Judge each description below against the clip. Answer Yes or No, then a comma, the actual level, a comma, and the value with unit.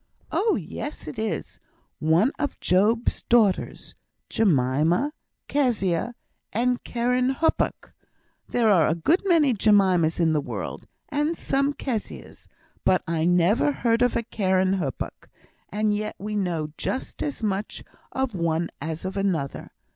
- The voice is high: Yes, high, 205 Hz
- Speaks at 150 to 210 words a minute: No, slow, 135 wpm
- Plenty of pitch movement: Yes, wide, 6.4 semitones